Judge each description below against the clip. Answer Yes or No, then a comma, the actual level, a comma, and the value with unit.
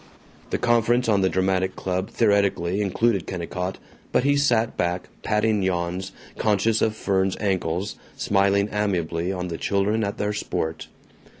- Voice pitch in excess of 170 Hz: No, low, 100 Hz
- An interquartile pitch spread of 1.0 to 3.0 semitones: Yes, narrow, 2.6 semitones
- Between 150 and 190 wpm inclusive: No, average, 140 wpm